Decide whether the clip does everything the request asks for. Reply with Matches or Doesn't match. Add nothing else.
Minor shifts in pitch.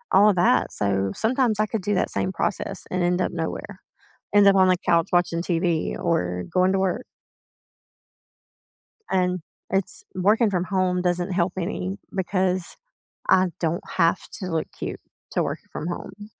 Matches